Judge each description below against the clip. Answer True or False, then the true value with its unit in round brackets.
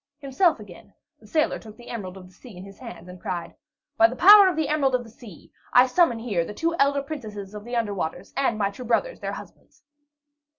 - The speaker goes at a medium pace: False (230 wpm)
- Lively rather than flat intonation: True (5.7 semitones)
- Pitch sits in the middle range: False (230 Hz)